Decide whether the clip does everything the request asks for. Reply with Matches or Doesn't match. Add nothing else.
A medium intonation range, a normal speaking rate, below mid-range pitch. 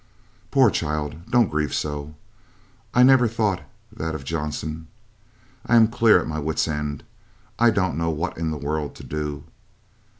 Doesn't match